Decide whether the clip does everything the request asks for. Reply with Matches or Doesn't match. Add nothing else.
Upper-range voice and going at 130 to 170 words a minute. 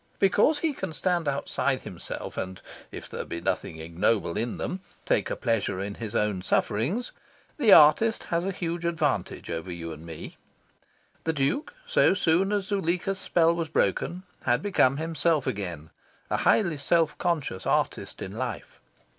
Doesn't match